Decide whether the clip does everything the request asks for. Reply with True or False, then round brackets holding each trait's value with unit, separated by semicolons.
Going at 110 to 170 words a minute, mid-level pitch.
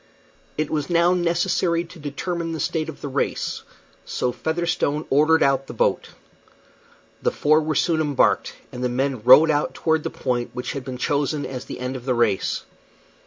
False (180 wpm; 145 Hz)